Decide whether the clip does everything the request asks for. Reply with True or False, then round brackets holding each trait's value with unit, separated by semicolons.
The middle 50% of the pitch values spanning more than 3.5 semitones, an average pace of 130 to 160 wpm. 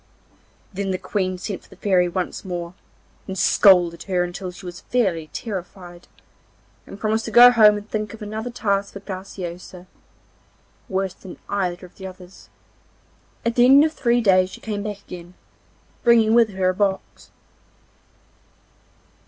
False (2.9 semitones; 155 wpm)